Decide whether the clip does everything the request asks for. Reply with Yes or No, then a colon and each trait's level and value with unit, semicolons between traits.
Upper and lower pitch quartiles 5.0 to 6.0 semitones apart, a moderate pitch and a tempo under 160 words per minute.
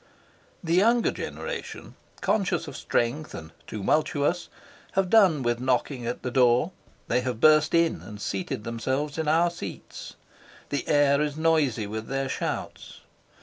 Yes: average, 5.3 semitones; medium, 145 Hz; average, 145 wpm